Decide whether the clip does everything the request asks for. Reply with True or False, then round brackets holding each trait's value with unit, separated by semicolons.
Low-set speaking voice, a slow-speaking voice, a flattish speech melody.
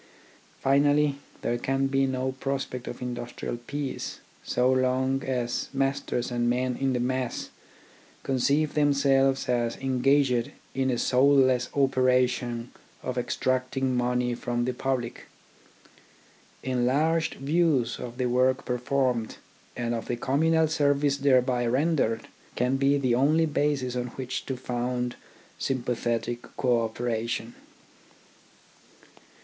True (130 Hz; 115 wpm; 1.9 semitones)